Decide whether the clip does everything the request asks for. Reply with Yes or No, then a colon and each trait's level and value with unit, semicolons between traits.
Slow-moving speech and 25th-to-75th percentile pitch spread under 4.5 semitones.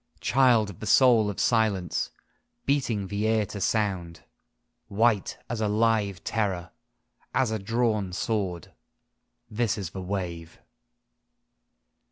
Yes: slow, 120 wpm; average, 3.0 semitones